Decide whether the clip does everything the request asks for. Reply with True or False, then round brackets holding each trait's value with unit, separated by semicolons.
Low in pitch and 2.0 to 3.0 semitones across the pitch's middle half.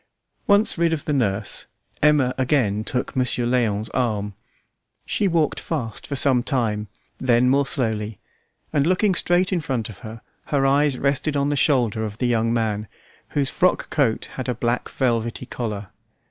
False (125 Hz; 4.3 semitones)